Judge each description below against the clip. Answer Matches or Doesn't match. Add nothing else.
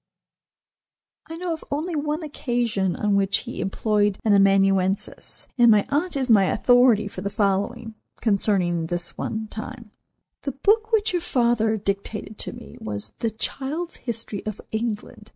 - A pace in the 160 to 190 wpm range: Doesn't match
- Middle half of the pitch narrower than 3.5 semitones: Doesn't match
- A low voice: Doesn't match